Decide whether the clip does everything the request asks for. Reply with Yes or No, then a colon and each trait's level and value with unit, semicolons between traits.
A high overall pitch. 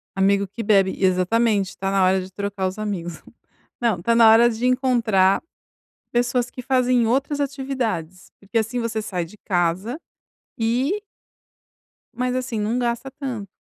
Yes: high, 225 Hz